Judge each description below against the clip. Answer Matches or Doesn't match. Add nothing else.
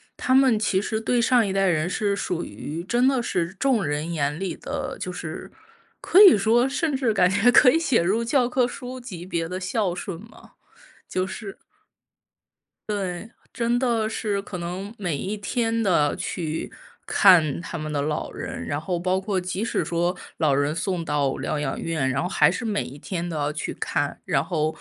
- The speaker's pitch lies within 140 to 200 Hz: Matches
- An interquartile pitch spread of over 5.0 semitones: Matches